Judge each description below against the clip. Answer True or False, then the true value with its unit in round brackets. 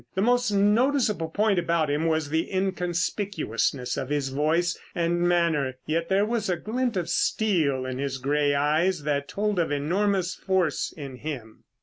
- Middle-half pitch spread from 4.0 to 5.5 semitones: True (5.2 semitones)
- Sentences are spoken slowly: False (160 wpm)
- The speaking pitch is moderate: True (170 Hz)